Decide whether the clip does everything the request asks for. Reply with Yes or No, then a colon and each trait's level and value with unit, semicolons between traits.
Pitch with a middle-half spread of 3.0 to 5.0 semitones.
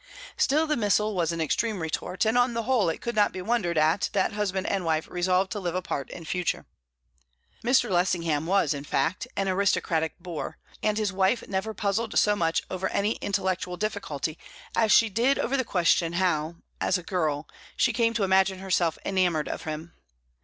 Yes: average, 4.0 semitones